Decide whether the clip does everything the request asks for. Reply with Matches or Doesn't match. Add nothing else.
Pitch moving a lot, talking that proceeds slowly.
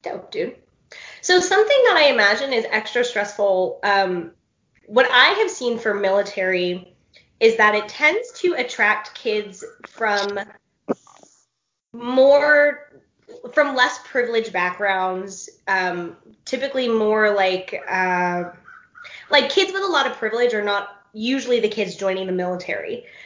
Matches